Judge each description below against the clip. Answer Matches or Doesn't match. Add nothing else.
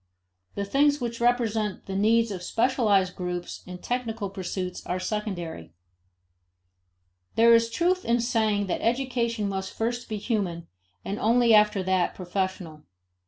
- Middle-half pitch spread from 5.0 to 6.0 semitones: Doesn't match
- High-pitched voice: Matches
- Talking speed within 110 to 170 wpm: Matches